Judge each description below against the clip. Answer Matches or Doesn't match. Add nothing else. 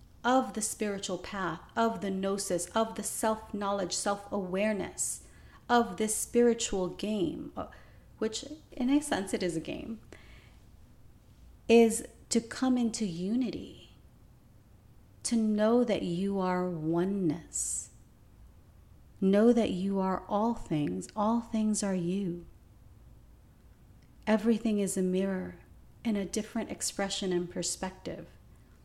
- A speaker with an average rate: Doesn't match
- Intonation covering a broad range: Doesn't match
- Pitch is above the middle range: Matches